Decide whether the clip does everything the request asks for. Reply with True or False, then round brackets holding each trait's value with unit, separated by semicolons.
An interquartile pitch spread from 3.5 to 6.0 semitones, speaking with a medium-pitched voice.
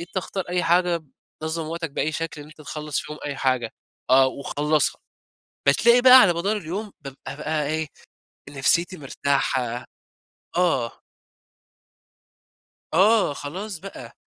True (4.0 semitones; 155 Hz)